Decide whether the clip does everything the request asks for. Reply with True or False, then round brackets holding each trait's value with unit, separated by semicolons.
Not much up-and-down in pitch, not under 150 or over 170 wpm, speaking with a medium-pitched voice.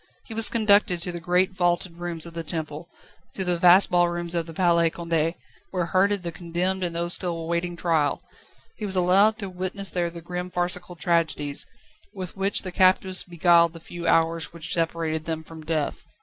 False (1.7 semitones; 190 wpm; 175 Hz)